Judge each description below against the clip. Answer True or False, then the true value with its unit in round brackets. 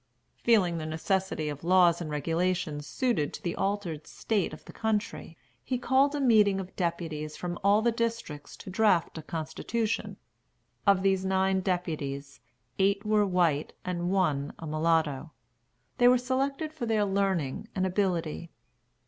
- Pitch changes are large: False (4.7 semitones)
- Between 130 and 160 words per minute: True (150 wpm)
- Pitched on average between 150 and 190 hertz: True (185 Hz)